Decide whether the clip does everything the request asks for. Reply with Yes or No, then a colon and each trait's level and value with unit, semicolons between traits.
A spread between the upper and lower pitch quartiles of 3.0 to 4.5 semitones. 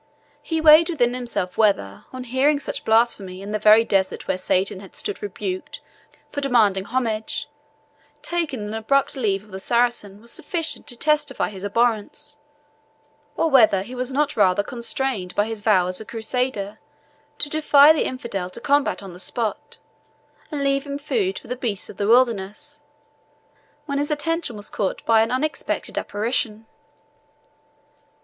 No: wide, 5.4 semitones